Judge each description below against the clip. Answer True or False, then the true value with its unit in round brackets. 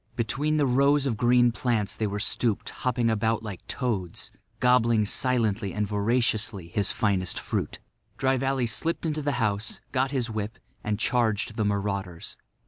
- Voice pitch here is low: True (115 Hz)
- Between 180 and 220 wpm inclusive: False (155 wpm)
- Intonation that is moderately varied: True (3.6 semitones)